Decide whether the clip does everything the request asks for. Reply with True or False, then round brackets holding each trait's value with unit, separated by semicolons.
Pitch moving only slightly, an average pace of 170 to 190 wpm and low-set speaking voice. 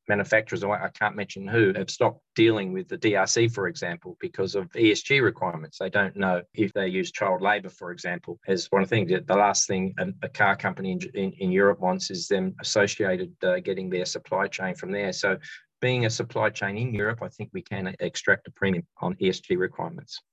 False (2.1 semitones; 200 wpm; 100 Hz)